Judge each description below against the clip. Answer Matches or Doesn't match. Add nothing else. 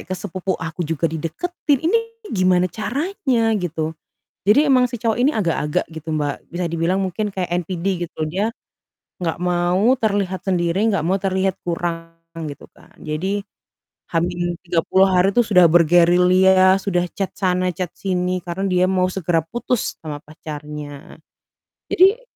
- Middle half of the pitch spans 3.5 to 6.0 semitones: Doesn't match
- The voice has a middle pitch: Matches